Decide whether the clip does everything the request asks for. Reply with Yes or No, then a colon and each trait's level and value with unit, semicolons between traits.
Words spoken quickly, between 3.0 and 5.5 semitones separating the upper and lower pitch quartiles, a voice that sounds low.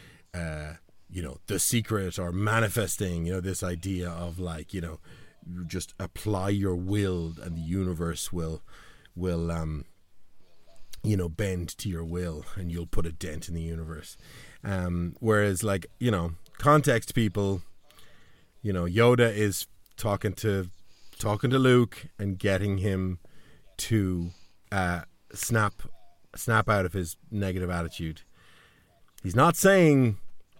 No: slow, 135 wpm; average, 3.4 semitones; very low, 95 Hz